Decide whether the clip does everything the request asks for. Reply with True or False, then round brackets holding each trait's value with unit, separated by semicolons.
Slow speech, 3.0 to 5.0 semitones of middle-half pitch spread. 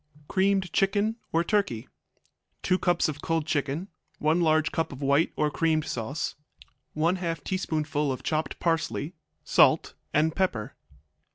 True (130 wpm; 3.4 semitones)